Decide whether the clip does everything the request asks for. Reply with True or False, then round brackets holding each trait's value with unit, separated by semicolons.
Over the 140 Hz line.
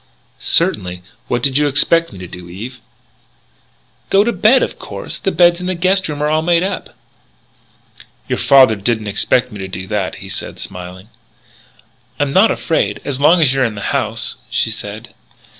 False (135 Hz)